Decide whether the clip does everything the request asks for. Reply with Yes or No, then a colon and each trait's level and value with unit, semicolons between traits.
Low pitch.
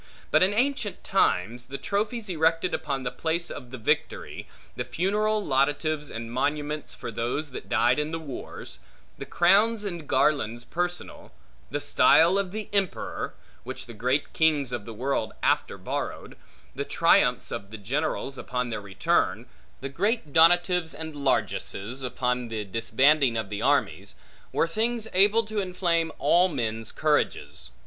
No: medium, 150 Hz